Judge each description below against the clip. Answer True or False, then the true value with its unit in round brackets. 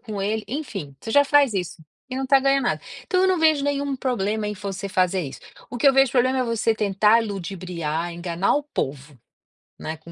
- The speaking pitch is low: False (215 Hz)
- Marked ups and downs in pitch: True (6.7 semitones)